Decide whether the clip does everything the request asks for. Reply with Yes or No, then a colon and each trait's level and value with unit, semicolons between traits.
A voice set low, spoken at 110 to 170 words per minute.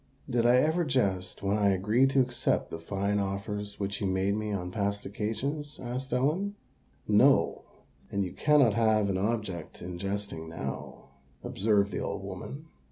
Yes: low, 105 Hz; average, 165 wpm